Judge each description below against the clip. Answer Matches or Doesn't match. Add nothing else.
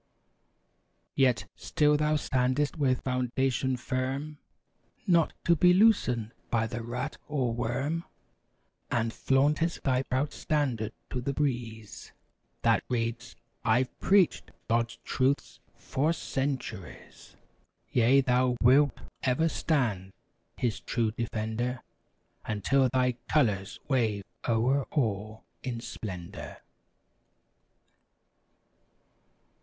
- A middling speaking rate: Doesn't match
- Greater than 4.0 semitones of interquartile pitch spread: Doesn't match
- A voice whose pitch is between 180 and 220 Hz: Doesn't match